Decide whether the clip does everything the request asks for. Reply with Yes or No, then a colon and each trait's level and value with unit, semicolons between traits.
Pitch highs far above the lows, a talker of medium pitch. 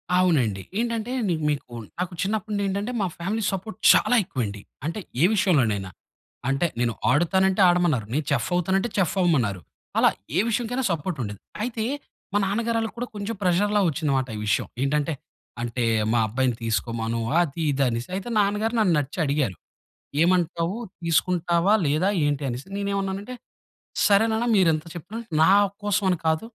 Yes: wide, 6.6 semitones; medium, 175 Hz